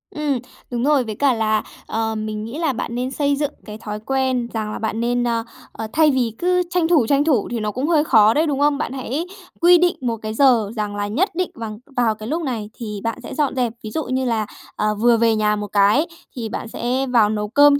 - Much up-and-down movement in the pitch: No, average, 4.7 semitones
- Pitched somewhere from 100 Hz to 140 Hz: No, high, 240 Hz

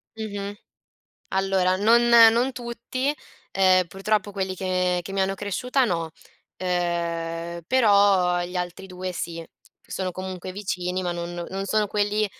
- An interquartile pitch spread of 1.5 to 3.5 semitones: Yes, narrow, 2.6 semitones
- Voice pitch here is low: No, high, 190 Hz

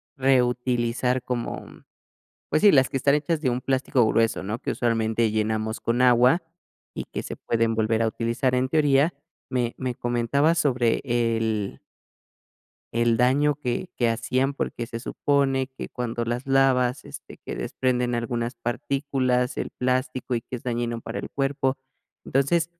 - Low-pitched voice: Yes, low, 125 Hz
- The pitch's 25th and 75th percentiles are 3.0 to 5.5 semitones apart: No, narrow, 2.4 semitones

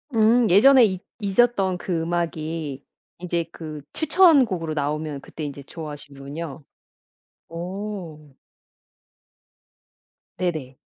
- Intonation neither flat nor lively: Yes, average, 4.5 semitones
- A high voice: No, medium, 165 Hz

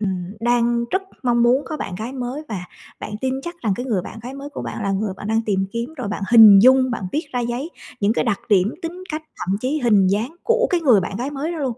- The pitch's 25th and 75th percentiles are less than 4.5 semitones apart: No, average, 4.9 semitones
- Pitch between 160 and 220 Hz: No, high, 240 Hz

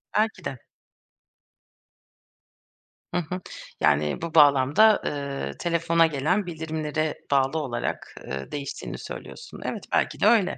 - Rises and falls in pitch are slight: No, average, 3.8 semitones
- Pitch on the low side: No, medium, 155 Hz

